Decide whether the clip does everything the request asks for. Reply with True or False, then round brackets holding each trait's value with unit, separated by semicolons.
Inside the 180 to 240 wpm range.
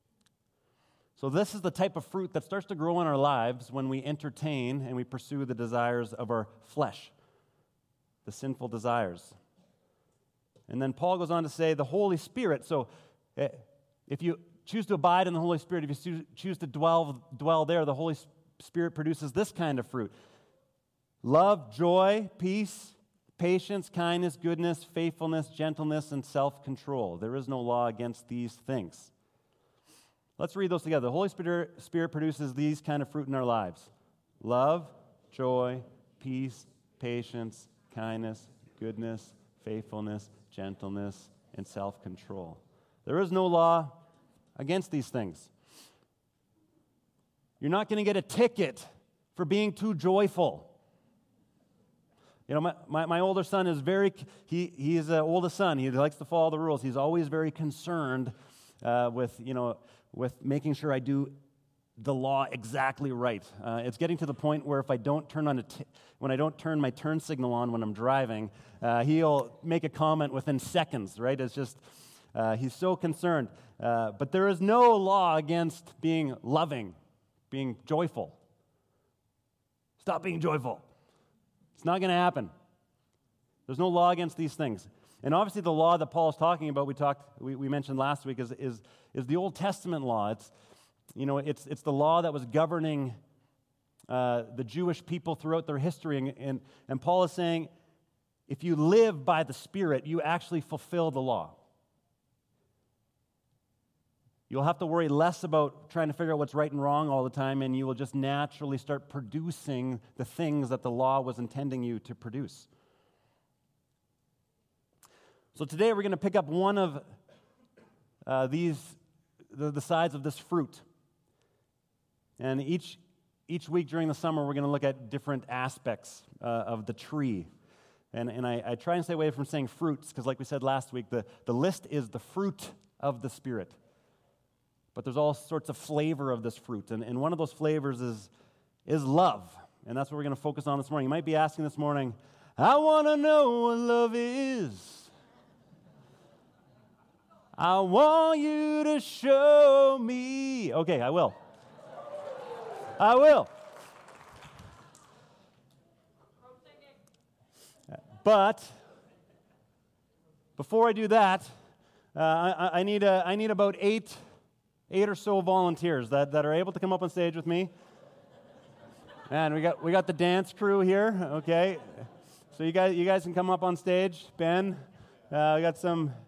False (165 wpm)